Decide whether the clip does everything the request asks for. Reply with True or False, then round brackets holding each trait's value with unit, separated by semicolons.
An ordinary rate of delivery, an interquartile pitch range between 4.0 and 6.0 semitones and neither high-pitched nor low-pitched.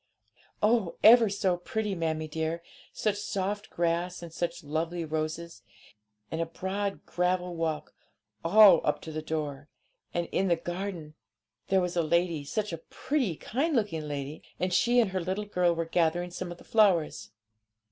False (165 wpm; 3.3 semitones; 175 Hz)